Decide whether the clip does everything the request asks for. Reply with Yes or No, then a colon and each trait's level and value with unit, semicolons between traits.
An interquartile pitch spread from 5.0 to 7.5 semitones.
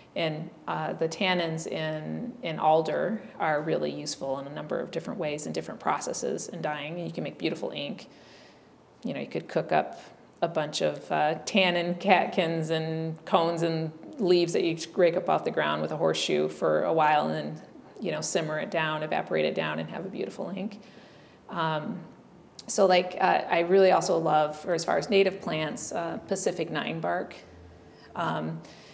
No: average, 3.1 semitones